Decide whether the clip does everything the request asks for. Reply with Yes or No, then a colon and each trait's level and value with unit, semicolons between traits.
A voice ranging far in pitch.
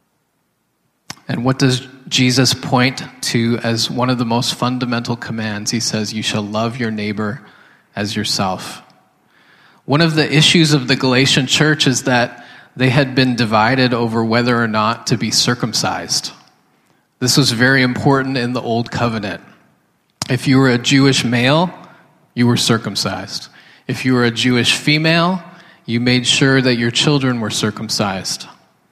No: average, 2.8 semitones